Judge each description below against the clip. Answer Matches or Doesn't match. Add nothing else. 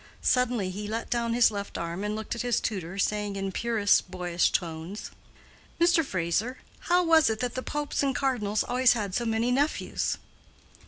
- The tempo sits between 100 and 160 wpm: Doesn't match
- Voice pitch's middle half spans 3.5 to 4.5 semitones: Matches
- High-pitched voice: Matches